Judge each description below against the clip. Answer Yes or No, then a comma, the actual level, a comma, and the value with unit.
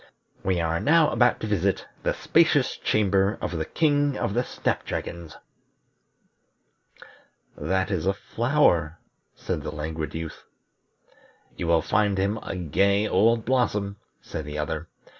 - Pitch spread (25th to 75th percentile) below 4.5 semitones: No, average, 5.2 semitones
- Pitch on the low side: Yes, very low, 95 Hz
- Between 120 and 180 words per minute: Yes, average, 140 wpm